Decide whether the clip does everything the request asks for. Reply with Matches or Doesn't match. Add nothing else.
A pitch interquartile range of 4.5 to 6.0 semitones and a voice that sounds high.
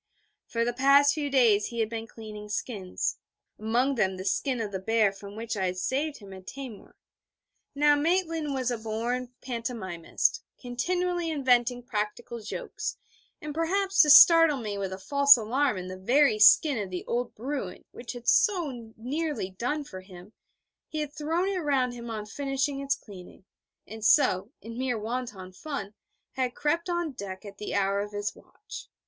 Matches